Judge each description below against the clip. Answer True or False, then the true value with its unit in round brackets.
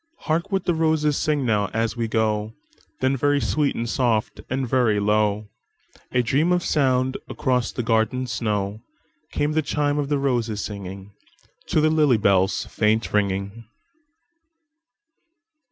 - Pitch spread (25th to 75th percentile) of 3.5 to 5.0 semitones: False (5.4 semitones)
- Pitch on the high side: False (120 Hz)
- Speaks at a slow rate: True (125 wpm)